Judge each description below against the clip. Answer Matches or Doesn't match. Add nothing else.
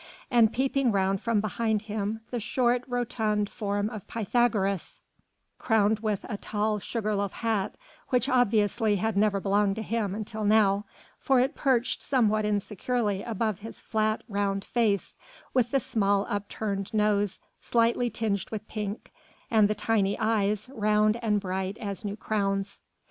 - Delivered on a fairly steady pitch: Matches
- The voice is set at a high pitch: Matches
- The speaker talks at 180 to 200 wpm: Doesn't match